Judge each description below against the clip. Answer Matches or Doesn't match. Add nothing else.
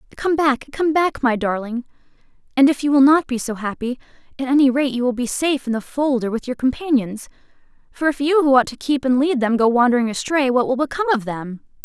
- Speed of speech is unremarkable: Doesn't match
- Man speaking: Doesn't match